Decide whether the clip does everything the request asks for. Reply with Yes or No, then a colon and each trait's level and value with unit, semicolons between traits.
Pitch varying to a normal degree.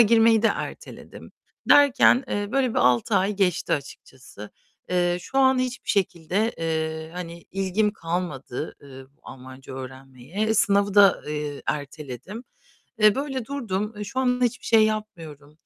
No: wide, 6.8 semitones